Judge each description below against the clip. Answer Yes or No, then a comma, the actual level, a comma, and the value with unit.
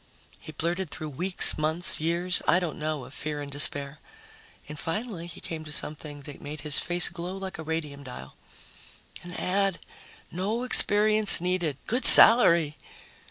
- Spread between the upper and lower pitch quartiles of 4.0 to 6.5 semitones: No, average, 3.6 semitones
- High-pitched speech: No, medium, 165 Hz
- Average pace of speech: Yes, average, 160 wpm